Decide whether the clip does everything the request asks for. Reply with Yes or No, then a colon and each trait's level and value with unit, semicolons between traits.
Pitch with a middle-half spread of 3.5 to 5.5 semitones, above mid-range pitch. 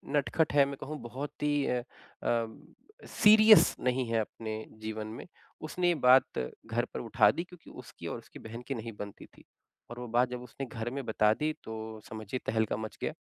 No: average, 4.0 semitones; low, 120 Hz